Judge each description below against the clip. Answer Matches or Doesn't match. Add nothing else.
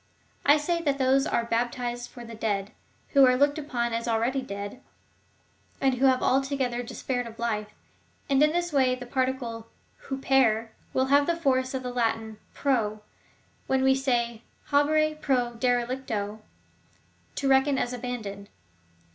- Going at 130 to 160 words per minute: Matches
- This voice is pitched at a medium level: Doesn't match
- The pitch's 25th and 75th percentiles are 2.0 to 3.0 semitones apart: Matches